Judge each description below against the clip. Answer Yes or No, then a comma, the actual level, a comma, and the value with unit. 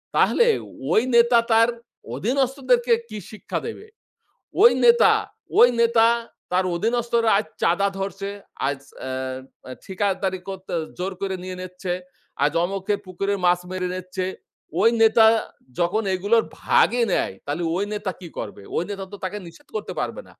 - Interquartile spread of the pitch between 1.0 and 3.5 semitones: No, average, 4.0 semitones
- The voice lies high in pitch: Yes, high, 200 Hz